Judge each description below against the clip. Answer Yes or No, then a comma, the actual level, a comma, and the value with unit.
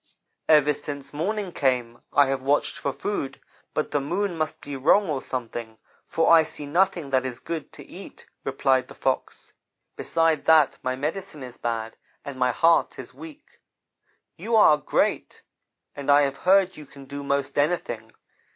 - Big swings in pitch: No, average, 3.8 semitones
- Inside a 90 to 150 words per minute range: No, average, 170 wpm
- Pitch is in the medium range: Yes, medium, 145 Hz